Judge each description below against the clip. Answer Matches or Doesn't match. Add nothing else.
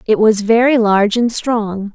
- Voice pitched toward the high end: Matches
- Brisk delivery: Doesn't match